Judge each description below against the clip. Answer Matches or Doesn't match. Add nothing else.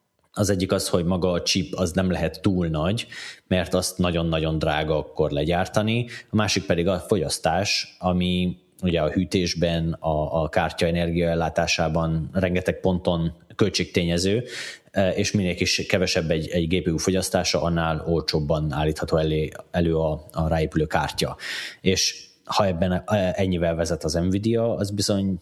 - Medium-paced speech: Matches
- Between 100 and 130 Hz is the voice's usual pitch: Doesn't match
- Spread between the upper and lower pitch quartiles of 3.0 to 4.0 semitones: Doesn't match